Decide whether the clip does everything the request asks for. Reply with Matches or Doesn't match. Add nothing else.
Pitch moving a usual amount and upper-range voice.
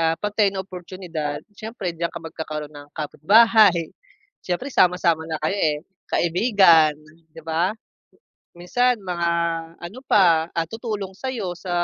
Doesn't match